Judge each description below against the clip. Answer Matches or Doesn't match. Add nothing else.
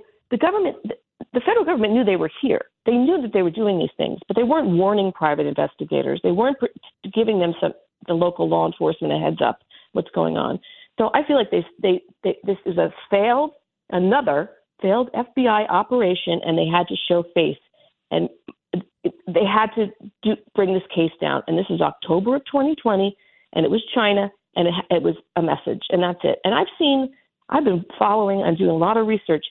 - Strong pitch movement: Matches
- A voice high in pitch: Matches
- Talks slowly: Doesn't match